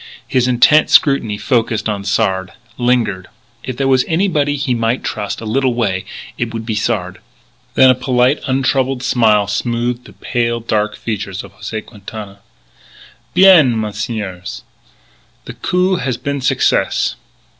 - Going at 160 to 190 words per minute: No, average, 140 wpm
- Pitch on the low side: Yes, low, 120 Hz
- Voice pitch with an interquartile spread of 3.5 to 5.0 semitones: Yes, average, 3.8 semitones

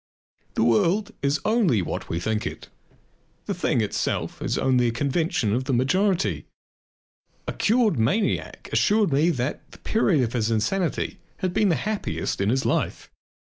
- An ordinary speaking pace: Yes, average, 160 wpm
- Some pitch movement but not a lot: No, wide, 8.7 semitones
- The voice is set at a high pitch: No, medium, 140 Hz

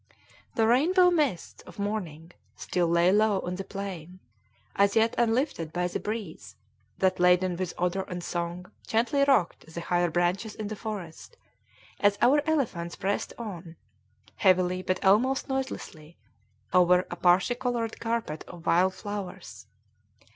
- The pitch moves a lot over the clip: No, average, 4.2 semitones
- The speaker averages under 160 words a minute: Yes, average, 140 wpm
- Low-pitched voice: No, high, 190 Hz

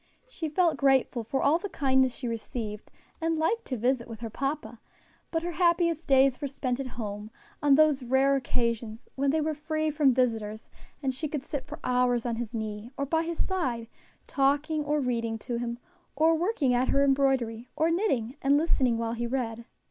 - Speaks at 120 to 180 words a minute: No, average, 195 wpm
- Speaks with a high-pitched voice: Yes, very high, 270 Hz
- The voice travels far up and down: No, average, 4.5 semitones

